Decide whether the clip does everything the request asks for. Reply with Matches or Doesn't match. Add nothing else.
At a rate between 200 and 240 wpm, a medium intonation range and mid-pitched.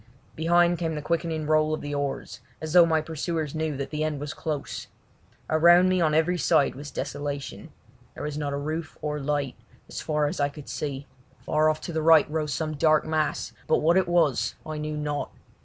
Doesn't match